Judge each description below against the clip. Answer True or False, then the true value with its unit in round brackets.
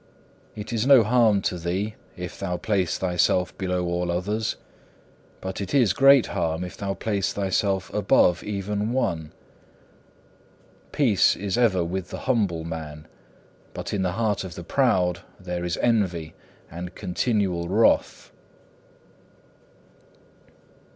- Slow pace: True (130 wpm)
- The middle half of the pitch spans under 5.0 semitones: True (3.3 semitones)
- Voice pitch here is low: True (95 Hz)